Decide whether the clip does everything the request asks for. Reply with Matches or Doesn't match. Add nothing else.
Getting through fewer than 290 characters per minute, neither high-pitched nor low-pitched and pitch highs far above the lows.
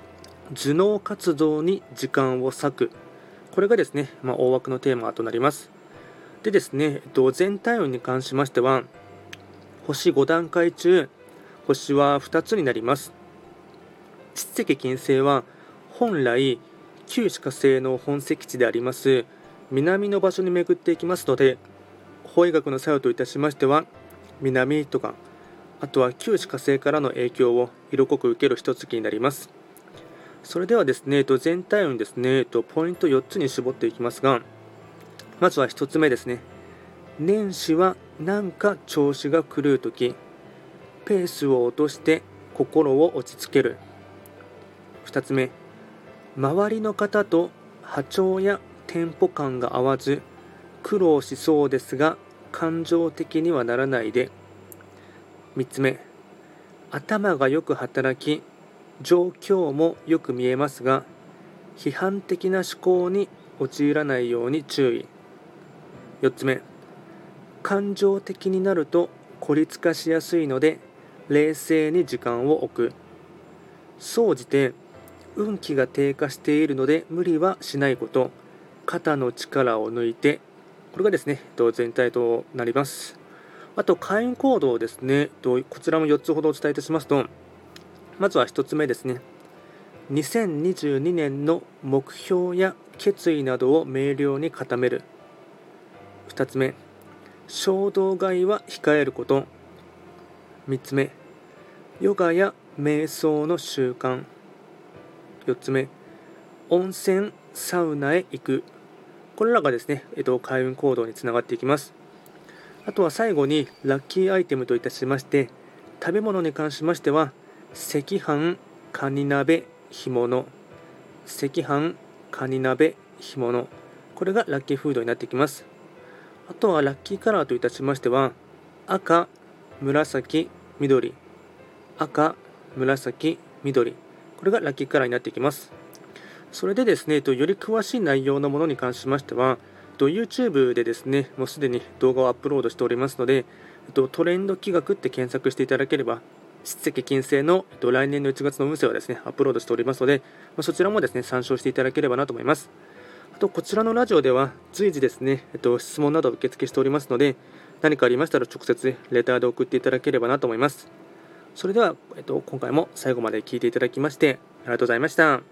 Doesn't match